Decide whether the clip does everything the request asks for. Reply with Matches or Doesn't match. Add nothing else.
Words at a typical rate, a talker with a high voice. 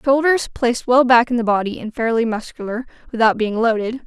Matches